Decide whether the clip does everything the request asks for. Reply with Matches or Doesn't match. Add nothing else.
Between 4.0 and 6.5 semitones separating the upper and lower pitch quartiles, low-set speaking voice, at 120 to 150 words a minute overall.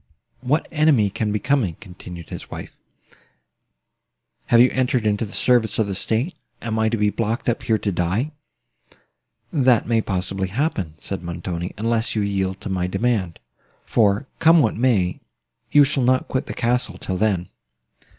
Doesn't match